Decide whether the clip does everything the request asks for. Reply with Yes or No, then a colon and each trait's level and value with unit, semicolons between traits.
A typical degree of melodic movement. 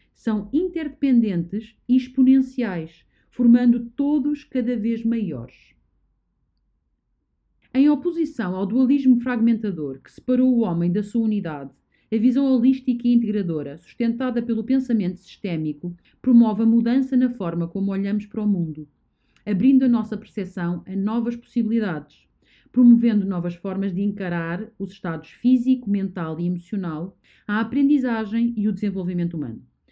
No: wide, 5.8 semitones